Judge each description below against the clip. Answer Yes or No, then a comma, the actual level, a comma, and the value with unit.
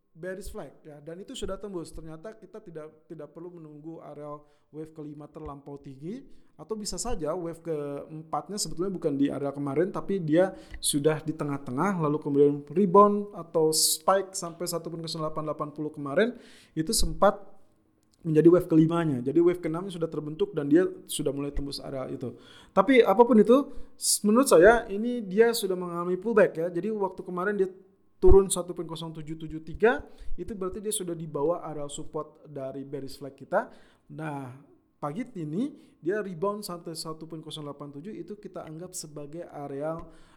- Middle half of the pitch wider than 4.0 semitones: Yes, average, 4.4 semitones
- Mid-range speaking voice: Yes, medium, 165 Hz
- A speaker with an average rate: No, fast, 145 wpm